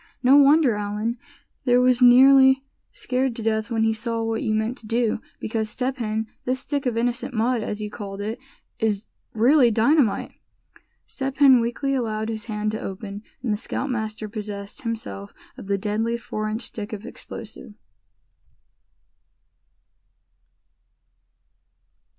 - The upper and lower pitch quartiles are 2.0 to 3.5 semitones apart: Yes, average, 2.8 semitones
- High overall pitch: Yes, high, 225 Hz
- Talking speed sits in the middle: Yes, average, 145 wpm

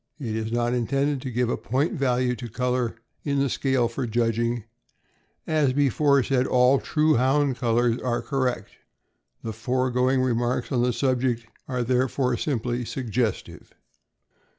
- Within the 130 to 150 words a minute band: Yes, average, 145 wpm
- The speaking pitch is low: Yes, low, 125 Hz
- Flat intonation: Yes, narrow, 2.0 semitones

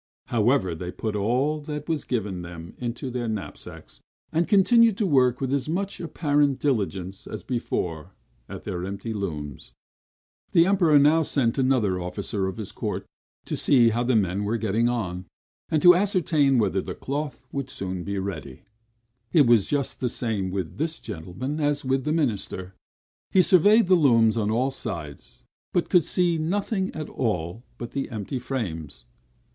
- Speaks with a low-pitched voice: Yes, low, 120 Hz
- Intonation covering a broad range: Yes, wide, 7.4 semitones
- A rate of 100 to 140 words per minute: No, average, 165 wpm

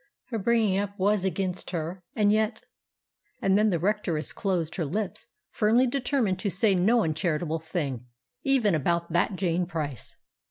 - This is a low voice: No, high, 190 Hz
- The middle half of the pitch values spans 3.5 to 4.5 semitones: Yes, average, 4.0 semitones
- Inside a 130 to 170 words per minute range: Yes, average, 155 wpm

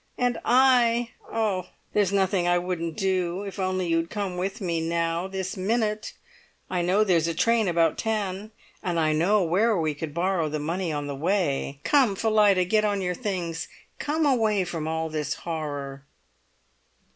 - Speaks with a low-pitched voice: No, medium, 185 Hz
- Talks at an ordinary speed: Yes, average, 170 wpm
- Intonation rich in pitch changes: No, average, 4.0 semitones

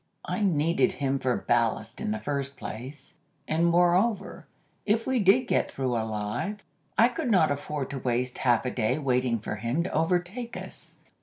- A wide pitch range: Yes, wide, 7.7 semitones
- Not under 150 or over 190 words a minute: Yes, average, 170 wpm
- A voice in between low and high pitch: Yes, medium, 145 Hz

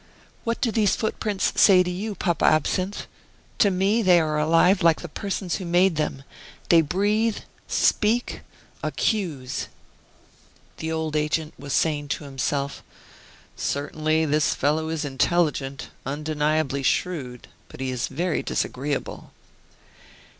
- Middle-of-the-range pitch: Yes, medium, 160 Hz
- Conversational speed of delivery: No, slow, 125 wpm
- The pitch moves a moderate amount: Yes, average, 4.3 semitones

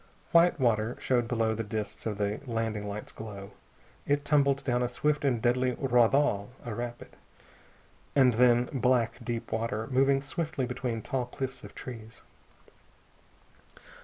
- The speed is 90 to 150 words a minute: Yes, average, 145 wpm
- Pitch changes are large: No, average, 3.0 semitones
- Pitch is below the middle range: Yes, low, 120 Hz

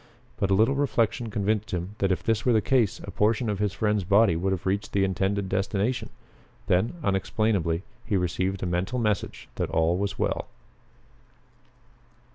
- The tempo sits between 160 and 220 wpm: Yes, average, 170 wpm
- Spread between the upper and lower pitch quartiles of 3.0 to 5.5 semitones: No, narrow, 2.5 semitones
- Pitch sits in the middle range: No, low, 100 Hz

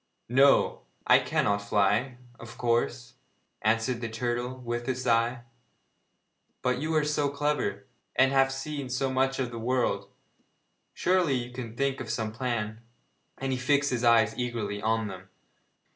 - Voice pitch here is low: Yes, low, 125 Hz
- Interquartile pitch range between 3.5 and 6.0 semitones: No, average, 2.9 semitones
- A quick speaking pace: No, average, 150 wpm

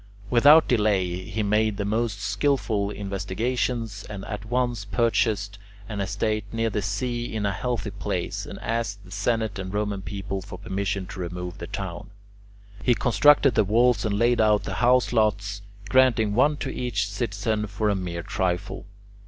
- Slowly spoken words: No, average, 165 wpm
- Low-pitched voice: Yes, low, 105 Hz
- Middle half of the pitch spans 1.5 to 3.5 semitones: Yes, average, 2.9 semitones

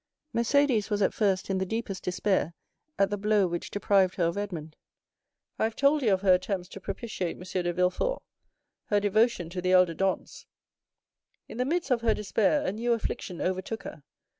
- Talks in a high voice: Yes, high, 195 Hz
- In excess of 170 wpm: Yes, average, 190 wpm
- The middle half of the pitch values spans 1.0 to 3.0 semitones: No, average, 3.4 semitones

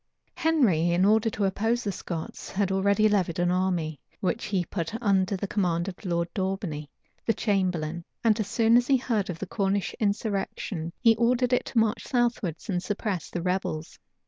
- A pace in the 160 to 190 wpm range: Yes, average, 180 wpm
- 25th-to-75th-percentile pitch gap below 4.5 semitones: Yes, average, 3.9 semitones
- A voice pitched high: Yes, high, 195 Hz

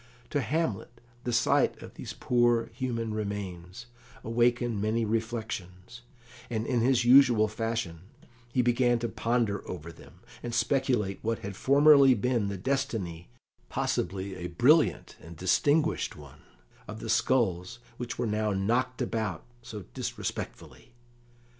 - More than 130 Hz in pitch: No, low, 115 Hz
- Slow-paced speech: Yes, slow, 130 wpm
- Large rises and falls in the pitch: No, average, 3.6 semitones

